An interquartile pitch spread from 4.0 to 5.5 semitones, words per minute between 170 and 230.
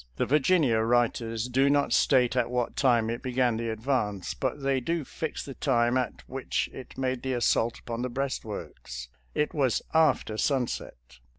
No: average, 2.8 semitones; average, 175 wpm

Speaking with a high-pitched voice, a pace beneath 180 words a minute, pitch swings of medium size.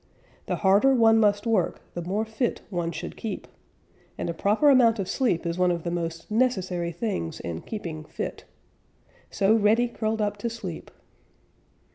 Yes: high, 205 Hz; average, 165 wpm; average, 4.5 semitones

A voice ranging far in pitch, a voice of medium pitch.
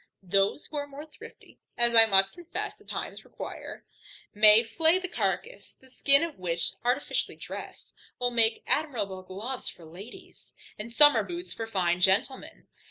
No: wide, 6.6 semitones; high, 230 Hz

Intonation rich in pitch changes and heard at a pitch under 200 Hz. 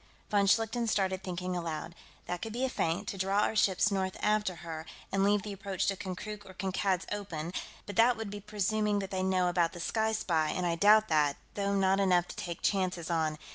No: average, 2.7 semitones; high, 190 Hz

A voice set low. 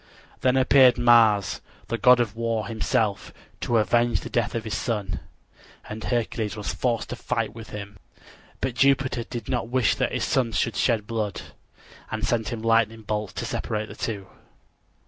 Yes: low, 115 Hz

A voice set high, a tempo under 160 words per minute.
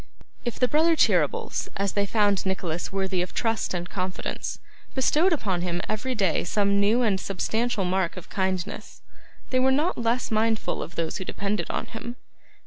No: high, 200 Hz; average, 170 wpm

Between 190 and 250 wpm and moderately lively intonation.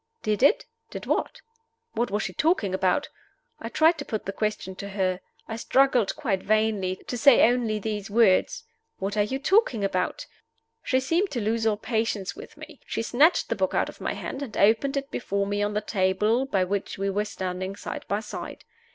Yes: average, 200 wpm; average, 3.9 semitones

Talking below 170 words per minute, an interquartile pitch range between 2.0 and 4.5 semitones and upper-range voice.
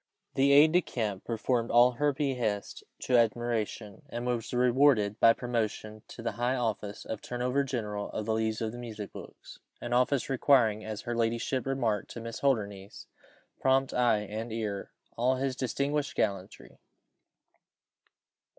No: average, 160 wpm; average, 3.1 semitones; low, 120 Hz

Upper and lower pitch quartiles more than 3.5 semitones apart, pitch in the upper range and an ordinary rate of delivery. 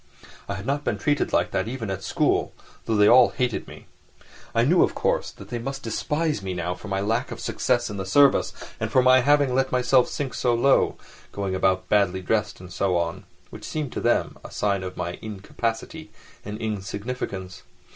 No: average, 5.0 semitones; low, 110 Hz; average, 195 wpm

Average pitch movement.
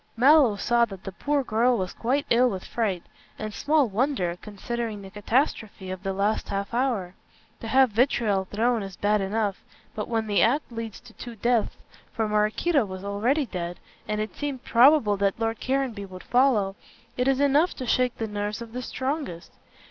Yes: average, 3.9 semitones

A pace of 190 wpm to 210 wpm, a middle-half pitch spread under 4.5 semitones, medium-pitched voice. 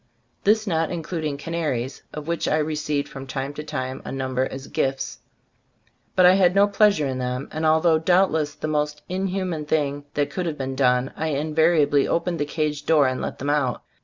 Yes: average, 200 wpm; average, 3.3 semitones; medium, 150 Hz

